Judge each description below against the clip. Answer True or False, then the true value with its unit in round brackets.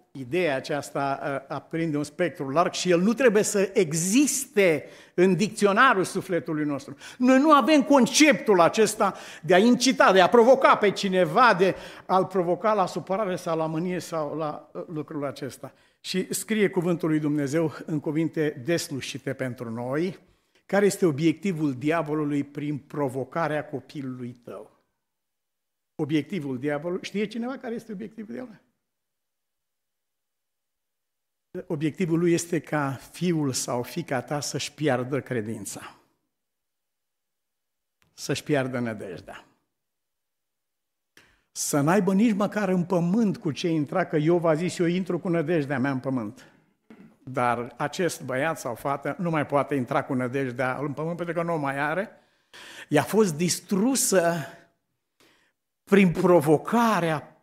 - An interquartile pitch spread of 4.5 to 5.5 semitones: True (4.9 semitones)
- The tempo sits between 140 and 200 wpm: False (130 wpm)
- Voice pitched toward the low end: False (165 Hz)